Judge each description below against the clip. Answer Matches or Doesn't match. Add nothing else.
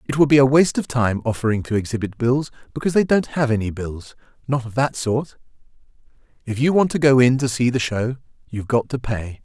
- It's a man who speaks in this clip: Matches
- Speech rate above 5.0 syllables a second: Matches